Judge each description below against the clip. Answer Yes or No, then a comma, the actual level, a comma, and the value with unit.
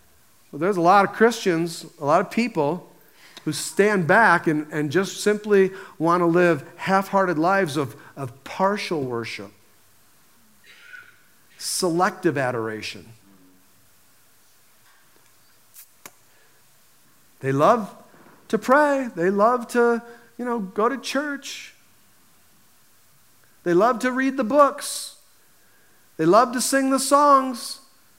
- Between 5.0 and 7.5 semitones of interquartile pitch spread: No, wide, 8.2 semitones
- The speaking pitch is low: No, high, 195 Hz